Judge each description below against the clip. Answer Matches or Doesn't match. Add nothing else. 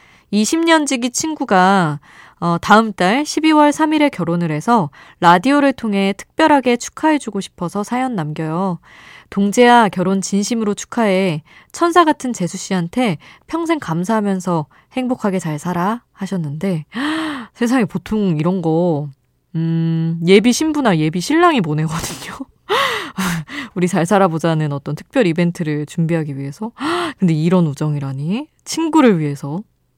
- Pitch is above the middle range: Matches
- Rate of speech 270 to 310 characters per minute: Matches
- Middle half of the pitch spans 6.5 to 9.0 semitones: Matches